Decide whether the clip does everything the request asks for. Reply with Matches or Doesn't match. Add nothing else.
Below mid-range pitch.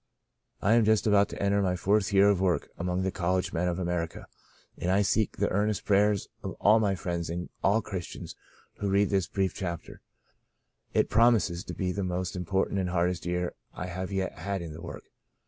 Matches